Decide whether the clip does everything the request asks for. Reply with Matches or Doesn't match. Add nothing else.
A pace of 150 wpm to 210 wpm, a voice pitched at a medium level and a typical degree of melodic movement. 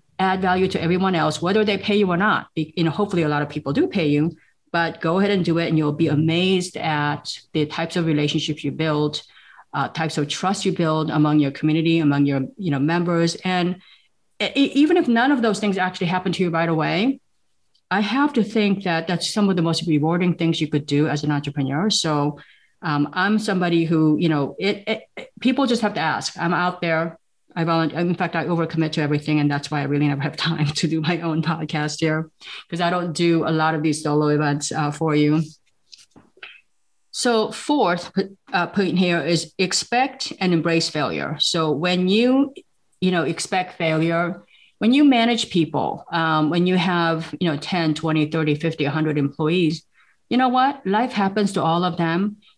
Matches